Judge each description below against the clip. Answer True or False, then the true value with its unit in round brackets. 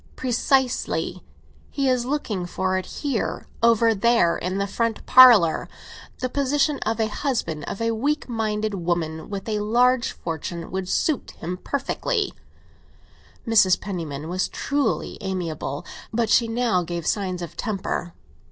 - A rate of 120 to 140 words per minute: True (135 wpm)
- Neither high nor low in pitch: False (215 Hz)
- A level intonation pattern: False (5.5 semitones)